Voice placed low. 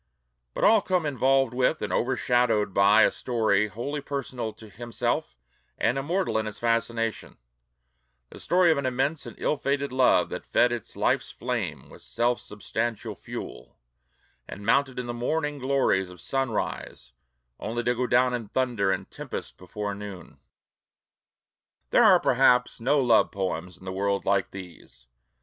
Yes: low, 120 Hz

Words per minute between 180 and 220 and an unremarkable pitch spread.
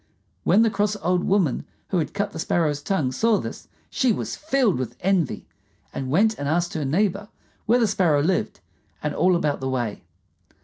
No: average, 185 wpm; wide, 6.0 semitones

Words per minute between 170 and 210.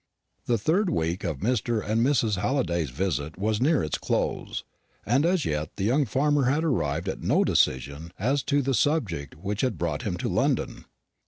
Yes: average, 180 wpm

